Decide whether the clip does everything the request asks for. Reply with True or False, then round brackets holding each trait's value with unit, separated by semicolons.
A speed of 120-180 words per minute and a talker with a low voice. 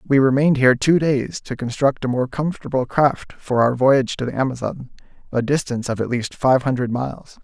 False (200 wpm; 130 Hz)